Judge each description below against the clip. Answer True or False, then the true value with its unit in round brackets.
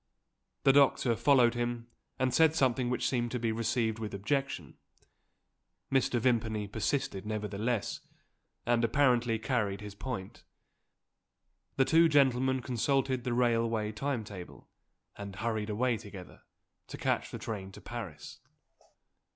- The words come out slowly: True (125 wpm)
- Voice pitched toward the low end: True (120 Hz)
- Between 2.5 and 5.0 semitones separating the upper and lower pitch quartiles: True (3.3 semitones)